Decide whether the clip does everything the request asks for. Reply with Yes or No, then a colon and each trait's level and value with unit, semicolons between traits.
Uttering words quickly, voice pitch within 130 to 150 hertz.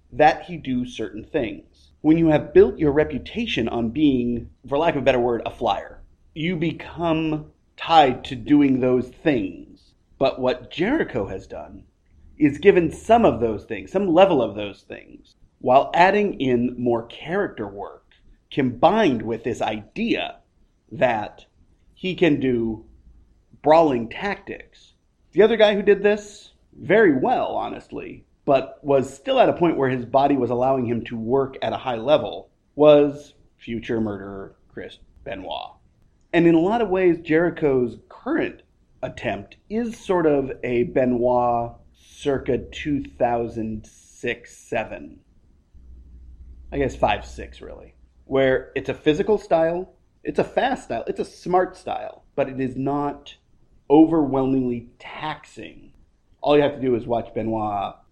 No: average, 145 wpm; low, 135 Hz